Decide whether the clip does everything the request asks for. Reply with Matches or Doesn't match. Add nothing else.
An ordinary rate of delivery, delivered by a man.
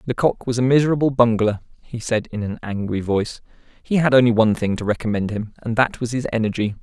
Doesn't match